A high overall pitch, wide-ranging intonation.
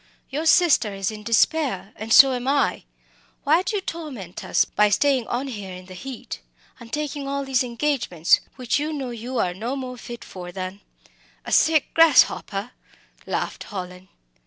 Yes: high, 245 Hz; wide, 6.0 semitones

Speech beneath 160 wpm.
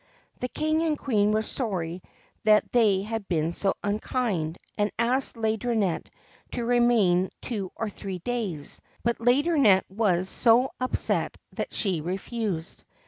Yes: average, 140 wpm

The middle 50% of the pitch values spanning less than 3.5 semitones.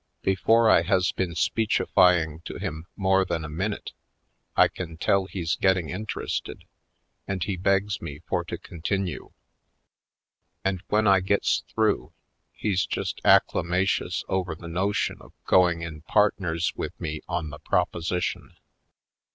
Yes: narrow, 2.6 semitones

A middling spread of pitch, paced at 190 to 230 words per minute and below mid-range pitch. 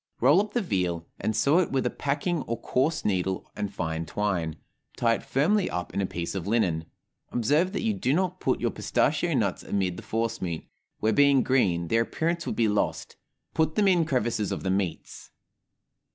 No: wide, 8.9 semitones; average, 195 wpm; low, 115 Hz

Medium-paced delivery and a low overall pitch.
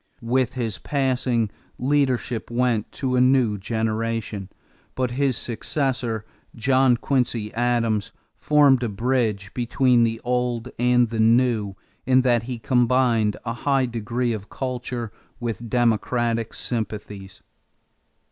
No: slow, 120 wpm; low, 120 Hz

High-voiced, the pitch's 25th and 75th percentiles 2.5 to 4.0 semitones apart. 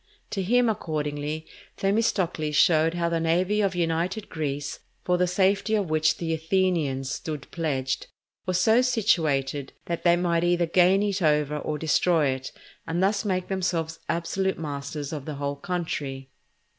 No: medium, 165 Hz; average, 3.7 semitones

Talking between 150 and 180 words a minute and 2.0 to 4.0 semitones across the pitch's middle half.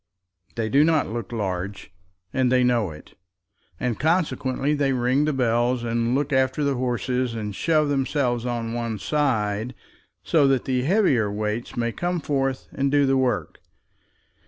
Yes: average, 155 wpm; average, 3.2 semitones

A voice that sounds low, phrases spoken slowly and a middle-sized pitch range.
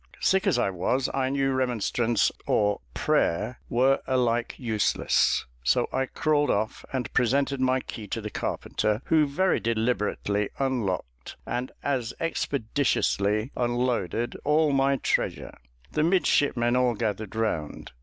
Yes: low, 125 Hz; slow, 130 wpm; average, 3.9 semitones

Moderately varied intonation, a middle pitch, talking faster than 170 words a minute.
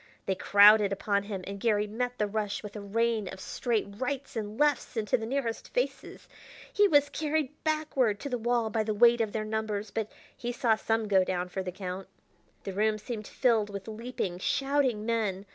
No: average, 3.1 semitones; high, 220 Hz; average, 195 wpm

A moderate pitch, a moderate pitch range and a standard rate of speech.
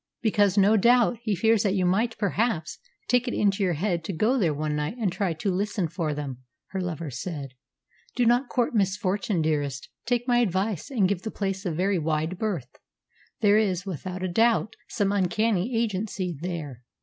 No: high, 195 Hz; average, 4.4 semitones; average, 185 wpm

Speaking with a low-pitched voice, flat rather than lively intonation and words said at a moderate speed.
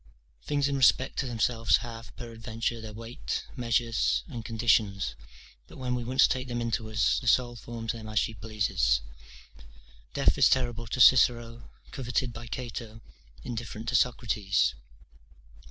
Yes: low, 115 Hz; narrow, 1.7 semitones; average, 145 wpm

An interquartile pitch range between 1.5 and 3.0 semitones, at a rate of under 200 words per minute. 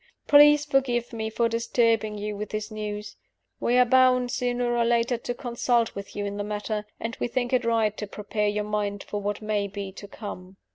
No: narrow, 2.6 semitones; fast, 205 wpm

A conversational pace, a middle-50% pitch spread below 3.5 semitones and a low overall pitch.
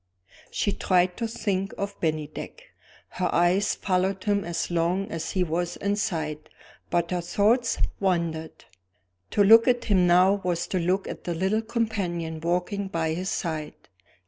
No: average, 155 wpm; average, 3.0 semitones; medium, 185 Hz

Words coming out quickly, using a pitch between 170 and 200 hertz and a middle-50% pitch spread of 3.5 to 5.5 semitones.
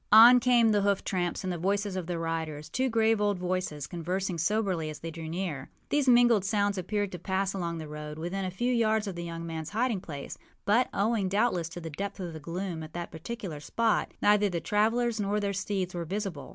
Yes: fast, 220 wpm; high, 190 Hz; average, 4.0 semitones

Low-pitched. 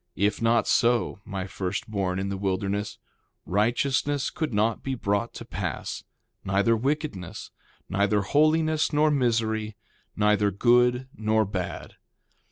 Yes: low, 110 Hz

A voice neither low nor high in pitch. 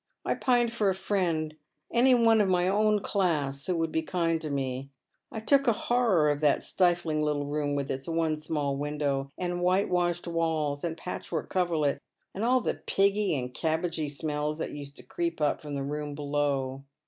Yes: medium, 160 Hz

